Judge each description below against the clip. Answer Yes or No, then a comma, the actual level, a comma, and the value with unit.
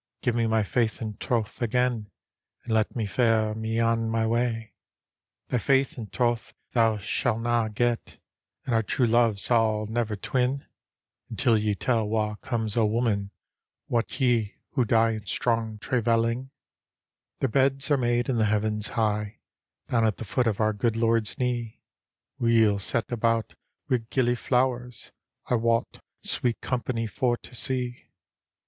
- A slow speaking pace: No, average, 160 wpm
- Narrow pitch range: Yes, narrow, 1.9 semitones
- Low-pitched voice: Yes, low, 115 Hz